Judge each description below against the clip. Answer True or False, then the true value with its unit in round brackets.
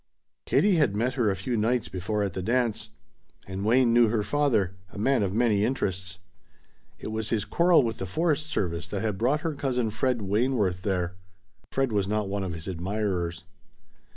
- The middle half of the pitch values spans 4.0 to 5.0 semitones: True (4.7 semitones)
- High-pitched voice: False (105 Hz)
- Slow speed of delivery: False (185 wpm)